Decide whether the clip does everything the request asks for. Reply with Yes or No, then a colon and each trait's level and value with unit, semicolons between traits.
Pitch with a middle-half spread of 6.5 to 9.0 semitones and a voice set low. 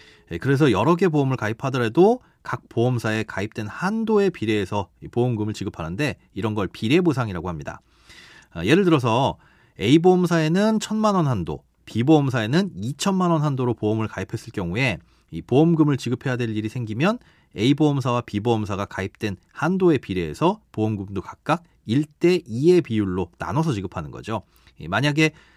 Yes: wide, 7.0 semitones; low, 125 Hz